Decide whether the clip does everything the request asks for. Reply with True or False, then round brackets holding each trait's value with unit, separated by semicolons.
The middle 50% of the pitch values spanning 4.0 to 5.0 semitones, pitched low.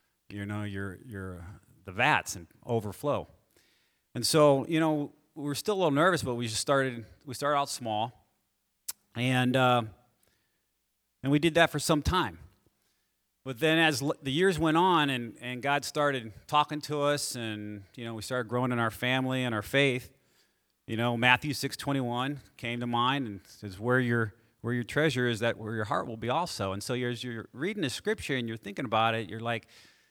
True (4.3 semitones; 125 Hz)